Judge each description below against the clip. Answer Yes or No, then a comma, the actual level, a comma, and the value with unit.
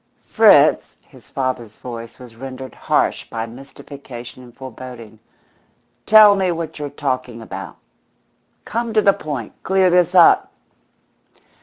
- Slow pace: Yes, slow, 125 wpm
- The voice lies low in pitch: Yes, low, 130 Hz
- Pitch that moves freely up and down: Yes, wide, 6.4 semitones